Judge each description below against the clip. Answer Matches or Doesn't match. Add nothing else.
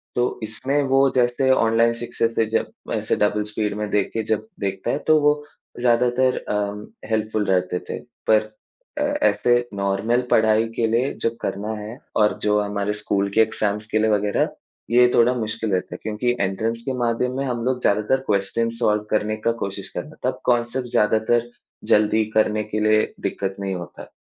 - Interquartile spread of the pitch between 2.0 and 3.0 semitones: Matches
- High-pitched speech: Doesn't match